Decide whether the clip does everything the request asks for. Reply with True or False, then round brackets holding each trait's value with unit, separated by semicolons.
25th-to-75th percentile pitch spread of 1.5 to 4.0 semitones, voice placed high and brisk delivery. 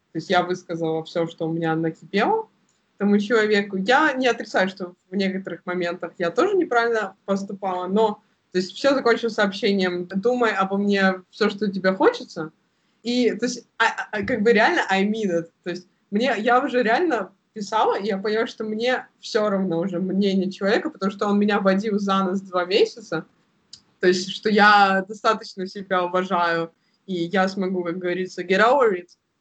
True (3.3 semitones; 195 Hz; 180 wpm)